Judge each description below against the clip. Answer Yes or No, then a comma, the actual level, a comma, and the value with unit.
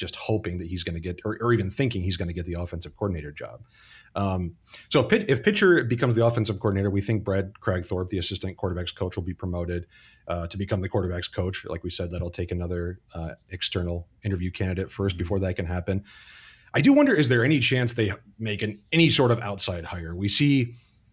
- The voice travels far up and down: No, average, 3.9 semitones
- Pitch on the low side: Yes, very low, 95 Hz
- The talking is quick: Yes, fast, 220 wpm